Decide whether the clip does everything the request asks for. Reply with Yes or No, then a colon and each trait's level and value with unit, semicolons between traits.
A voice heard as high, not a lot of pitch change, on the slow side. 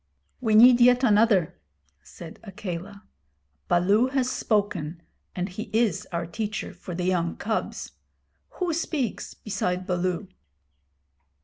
No: high, 205 Hz; average, 4.4 semitones; slow, 115 wpm